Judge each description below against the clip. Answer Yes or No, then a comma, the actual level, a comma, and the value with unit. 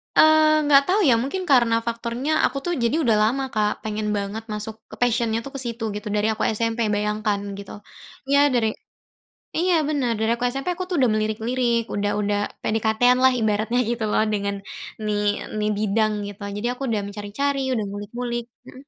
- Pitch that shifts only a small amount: No, average, 3.3 semitones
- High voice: Yes, high, 230 Hz